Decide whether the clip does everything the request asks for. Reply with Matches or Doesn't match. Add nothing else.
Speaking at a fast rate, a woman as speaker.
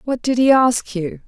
Matches